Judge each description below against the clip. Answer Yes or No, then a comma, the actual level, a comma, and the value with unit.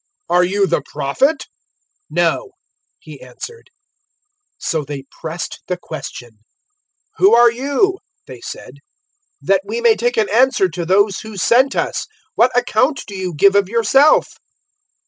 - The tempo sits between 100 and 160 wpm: Yes, average, 145 wpm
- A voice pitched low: No, high, 205 Hz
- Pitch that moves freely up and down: Yes, wide, 6.3 semitones